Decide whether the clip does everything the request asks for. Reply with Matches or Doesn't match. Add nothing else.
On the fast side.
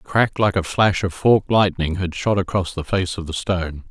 Matches